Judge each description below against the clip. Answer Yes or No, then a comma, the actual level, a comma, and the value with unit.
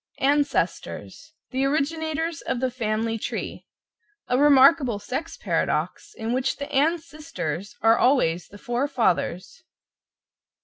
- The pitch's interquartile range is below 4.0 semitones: No, average, 4.7 semitones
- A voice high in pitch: Yes, very high, 265 Hz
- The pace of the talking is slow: Yes, slow, 120 wpm